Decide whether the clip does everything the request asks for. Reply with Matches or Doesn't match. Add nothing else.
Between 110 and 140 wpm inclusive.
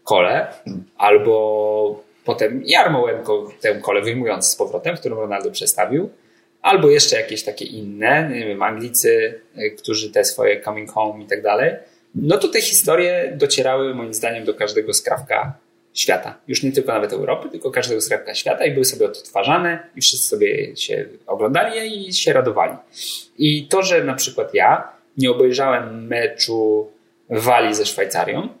Doesn't match